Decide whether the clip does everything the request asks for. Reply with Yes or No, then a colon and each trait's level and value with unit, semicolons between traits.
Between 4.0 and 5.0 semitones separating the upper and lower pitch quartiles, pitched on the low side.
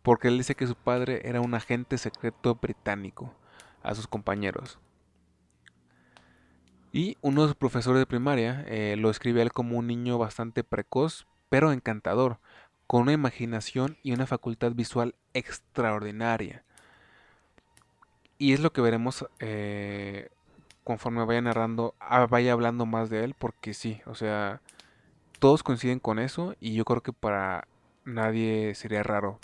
No: average, 2.7 semitones; low, 115 Hz